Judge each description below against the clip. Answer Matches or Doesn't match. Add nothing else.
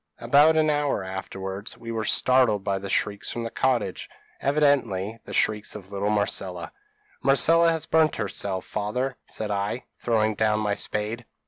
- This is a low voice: Matches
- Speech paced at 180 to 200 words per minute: Doesn't match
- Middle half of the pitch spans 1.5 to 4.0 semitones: Doesn't match